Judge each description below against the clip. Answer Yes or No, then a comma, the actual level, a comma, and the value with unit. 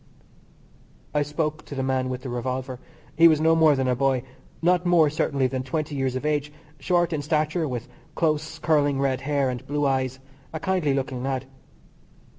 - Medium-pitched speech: Yes, medium, 145 Hz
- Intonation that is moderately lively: Yes, average, 3.0 semitones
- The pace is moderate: Yes, average, 185 wpm